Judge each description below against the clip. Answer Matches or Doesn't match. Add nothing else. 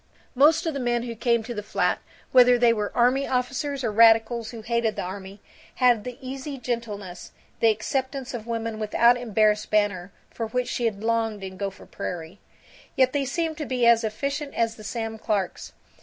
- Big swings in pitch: Doesn't match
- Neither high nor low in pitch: Doesn't match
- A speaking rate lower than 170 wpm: Doesn't match